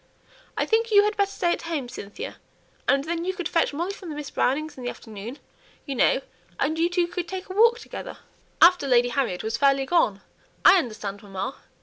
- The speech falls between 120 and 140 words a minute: No, fast, 205 wpm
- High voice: Yes, very high, 305 Hz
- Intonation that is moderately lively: No, wide, 6.6 semitones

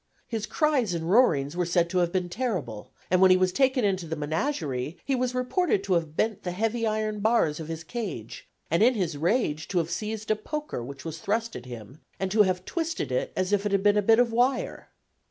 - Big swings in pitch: Yes, wide, 5.7 semitones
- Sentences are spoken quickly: Yes, fast, 230 wpm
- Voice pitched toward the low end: No, high, 190 Hz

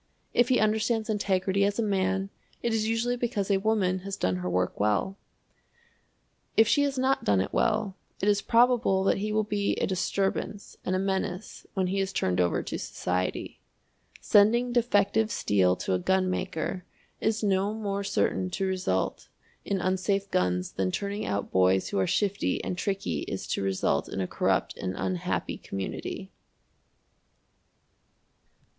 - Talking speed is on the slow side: No, average, 160 wpm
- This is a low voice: No, high, 195 Hz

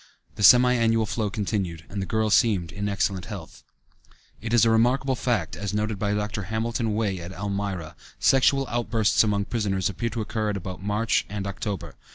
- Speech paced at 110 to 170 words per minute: No, average, 190 wpm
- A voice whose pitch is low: Yes, low, 105 Hz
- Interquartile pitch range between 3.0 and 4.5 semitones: No, narrow, 2.5 semitones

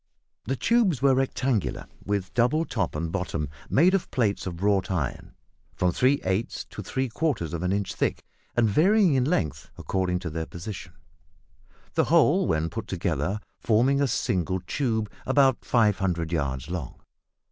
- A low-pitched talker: Yes, low, 100 Hz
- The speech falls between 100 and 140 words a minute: No, average, 160 wpm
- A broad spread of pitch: Yes, wide, 7.3 semitones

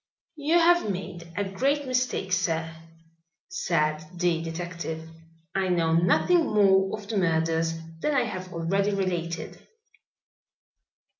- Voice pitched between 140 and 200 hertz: Yes, medium, 185 Hz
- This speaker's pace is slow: Yes, slow, 120 wpm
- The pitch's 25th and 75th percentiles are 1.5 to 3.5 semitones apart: No, average, 4.2 semitones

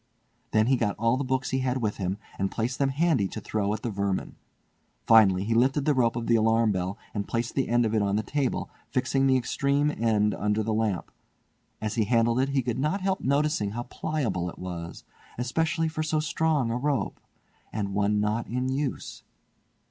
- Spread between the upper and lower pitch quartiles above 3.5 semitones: Yes, average, 4.3 semitones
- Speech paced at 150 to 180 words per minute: No, fast, 205 wpm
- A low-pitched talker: Yes, low, 115 Hz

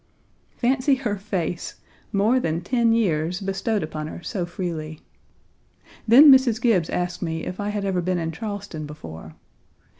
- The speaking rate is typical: Yes, average, 150 wpm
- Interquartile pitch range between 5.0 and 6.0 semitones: Yes, wide, 5.4 semitones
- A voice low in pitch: No, high, 190 Hz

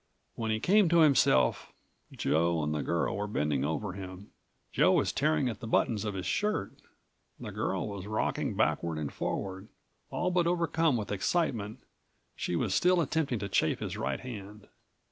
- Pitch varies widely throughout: Yes, wide, 7.1 semitones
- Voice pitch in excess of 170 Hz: No, low, 105 Hz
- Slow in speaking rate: No, average, 170 wpm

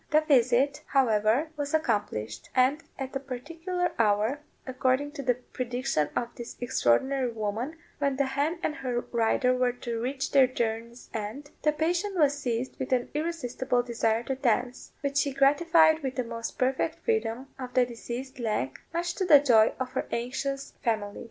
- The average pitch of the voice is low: No, very high, 260 Hz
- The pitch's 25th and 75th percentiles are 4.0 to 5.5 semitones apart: No, average, 3.5 semitones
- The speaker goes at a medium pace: Yes, average, 170 wpm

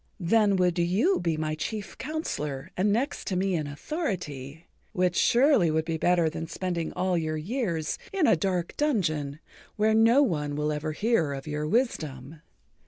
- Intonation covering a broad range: Yes, wide, 5.8 semitones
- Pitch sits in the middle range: Yes, medium, 175 Hz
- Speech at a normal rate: Yes, average, 170 wpm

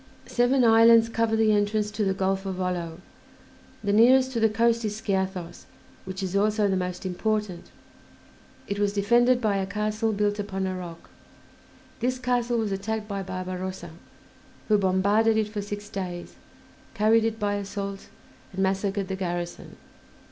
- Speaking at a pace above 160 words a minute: No, average, 155 wpm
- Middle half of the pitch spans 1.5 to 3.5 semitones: Yes, average, 2.7 semitones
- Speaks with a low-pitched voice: No, high, 205 Hz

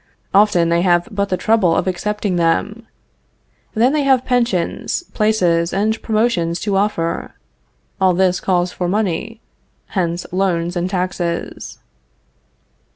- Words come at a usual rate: No, slow, 125 wpm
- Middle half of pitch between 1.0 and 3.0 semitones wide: No, average, 3.6 semitones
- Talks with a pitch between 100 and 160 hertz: No, medium, 185 Hz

